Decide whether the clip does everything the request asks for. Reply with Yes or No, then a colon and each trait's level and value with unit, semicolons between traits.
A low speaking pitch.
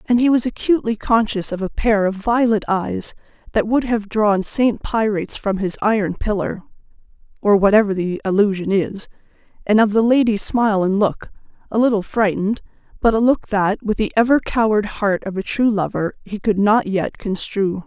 No: high, 210 Hz